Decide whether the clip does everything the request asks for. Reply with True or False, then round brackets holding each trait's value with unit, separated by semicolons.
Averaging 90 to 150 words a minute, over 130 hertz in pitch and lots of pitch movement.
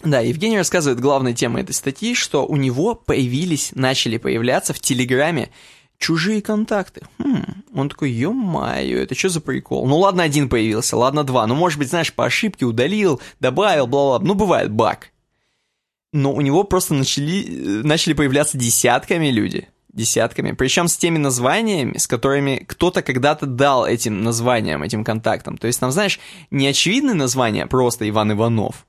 False (160 wpm; 140 Hz; 5.7 semitones)